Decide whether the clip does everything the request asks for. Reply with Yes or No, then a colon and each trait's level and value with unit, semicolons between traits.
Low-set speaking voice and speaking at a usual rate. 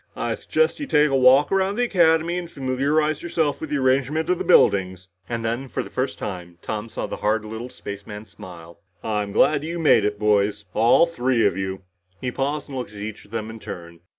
No: low, 125 Hz; fast, 215 wpm